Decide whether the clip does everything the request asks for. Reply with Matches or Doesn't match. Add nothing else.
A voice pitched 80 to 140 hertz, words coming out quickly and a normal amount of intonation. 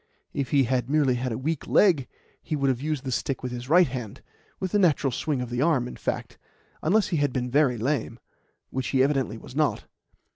Matches